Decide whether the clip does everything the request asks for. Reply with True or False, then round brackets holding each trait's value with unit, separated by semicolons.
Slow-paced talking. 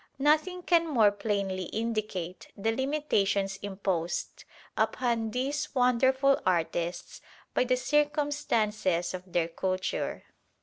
True (100 wpm)